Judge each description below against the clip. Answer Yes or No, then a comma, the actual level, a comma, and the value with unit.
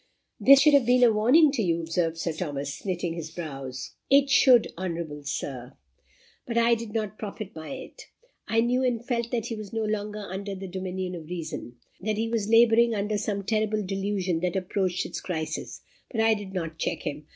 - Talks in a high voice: Yes, high, 200 Hz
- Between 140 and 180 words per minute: No, average, 195 wpm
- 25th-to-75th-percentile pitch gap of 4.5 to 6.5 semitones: Yes, average, 5.0 semitones